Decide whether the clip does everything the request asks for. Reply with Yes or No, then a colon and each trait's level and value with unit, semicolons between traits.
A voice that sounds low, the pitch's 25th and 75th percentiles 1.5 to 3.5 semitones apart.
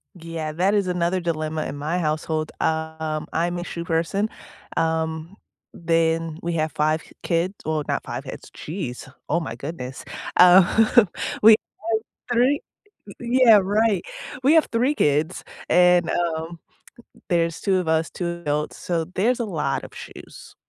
No: medium, 170 Hz; average, 2.8 semitones